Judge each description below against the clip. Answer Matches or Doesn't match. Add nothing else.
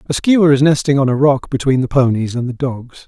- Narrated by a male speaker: Matches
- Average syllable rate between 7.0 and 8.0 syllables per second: Doesn't match